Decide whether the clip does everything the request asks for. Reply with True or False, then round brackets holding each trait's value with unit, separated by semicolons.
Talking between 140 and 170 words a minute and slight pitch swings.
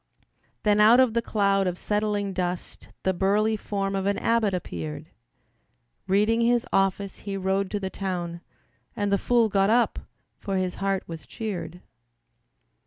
True (155 wpm; 2.1 semitones)